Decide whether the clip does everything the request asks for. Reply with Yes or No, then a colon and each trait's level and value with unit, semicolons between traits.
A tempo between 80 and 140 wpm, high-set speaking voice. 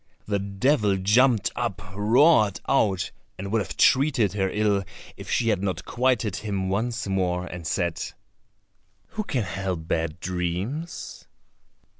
No: slow, 135 wpm; low, 100 Hz